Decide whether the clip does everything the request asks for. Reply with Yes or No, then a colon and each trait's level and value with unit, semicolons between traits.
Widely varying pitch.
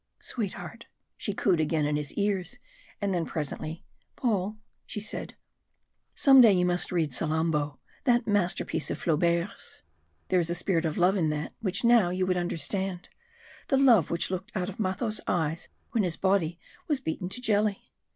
No: average, 3.8 semitones